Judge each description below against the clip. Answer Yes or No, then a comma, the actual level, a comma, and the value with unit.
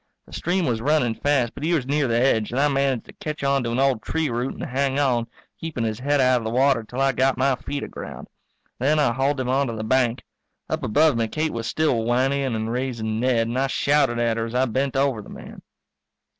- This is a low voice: Yes, low, 130 Hz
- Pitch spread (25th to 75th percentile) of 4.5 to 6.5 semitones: No, average, 3.0 semitones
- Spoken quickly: Yes, fast, 240 wpm